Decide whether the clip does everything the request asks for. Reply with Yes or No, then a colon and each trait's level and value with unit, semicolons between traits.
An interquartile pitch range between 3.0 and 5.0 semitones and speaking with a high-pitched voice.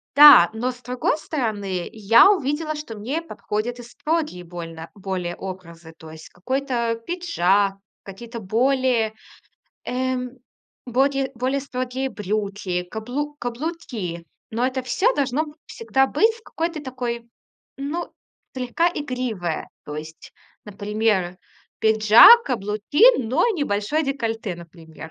No: wide, 5.6 semitones; high, 240 Hz